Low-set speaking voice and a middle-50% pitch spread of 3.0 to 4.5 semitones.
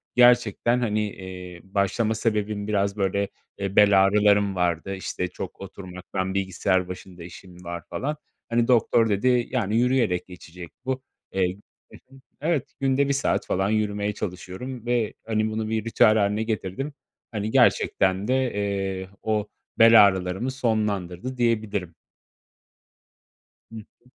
Yes: low, 105 Hz; average, 3.5 semitones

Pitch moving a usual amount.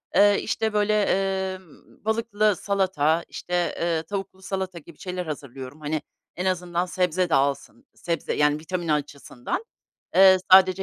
Yes: average, 3.6 semitones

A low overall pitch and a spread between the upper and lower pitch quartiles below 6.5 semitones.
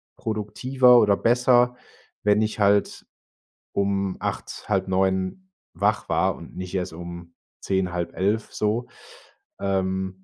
Yes: low, 100 Hz; average, 2.7 semitones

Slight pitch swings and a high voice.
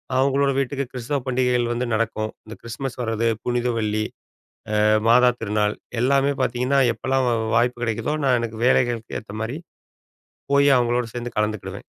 No: narrow, 2.3 semitones; low, 120 Hz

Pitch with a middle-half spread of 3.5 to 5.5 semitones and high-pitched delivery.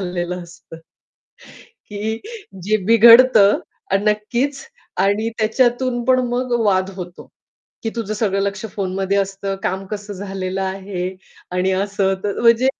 No: average, 2.8 semitones; high, 200 Hz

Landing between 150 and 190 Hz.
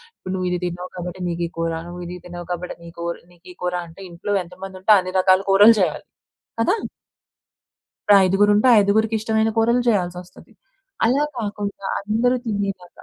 Yes: medium, 185 Hz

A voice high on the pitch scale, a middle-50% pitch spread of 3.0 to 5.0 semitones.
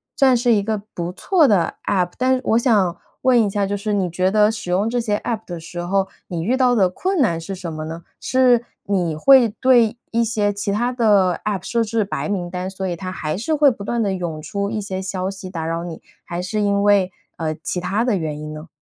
Yes: high, 200 Hz; average, 4.2 semitones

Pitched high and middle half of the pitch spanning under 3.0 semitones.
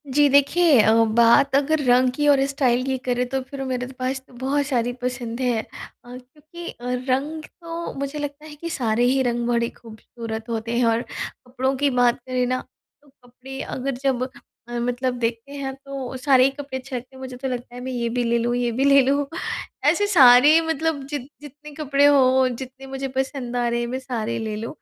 Yes: very high, 255 Hz; narrow, 2.4 semitones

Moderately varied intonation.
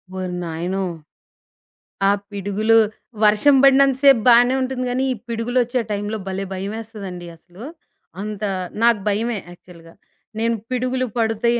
Yes: average, 3.9 semitones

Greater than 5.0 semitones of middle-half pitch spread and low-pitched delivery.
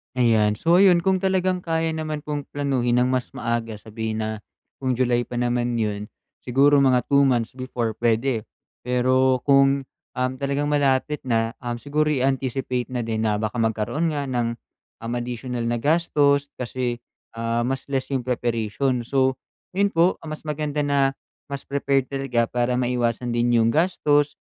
No: average, 3.1 semitones; low, 130 Hz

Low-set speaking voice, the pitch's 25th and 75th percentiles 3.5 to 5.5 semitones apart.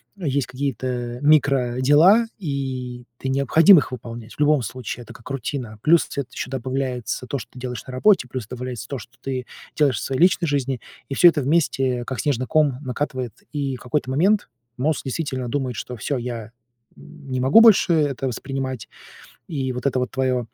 No: low, 130 Hz; narrow, 2.6 semitones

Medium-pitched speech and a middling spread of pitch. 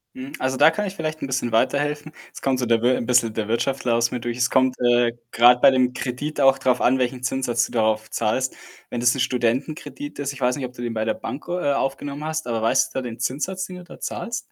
No: low, 130 Hz; average, 3.1 semitones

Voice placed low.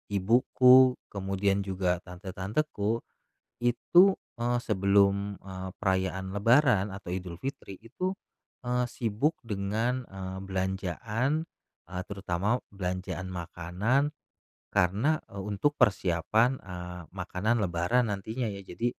Yes: low, 100 Hz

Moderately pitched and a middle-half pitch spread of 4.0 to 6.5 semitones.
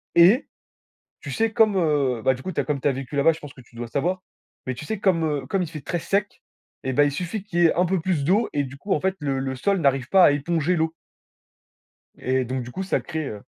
Yes: medium, 155 Hz; wide, 5.6 semitones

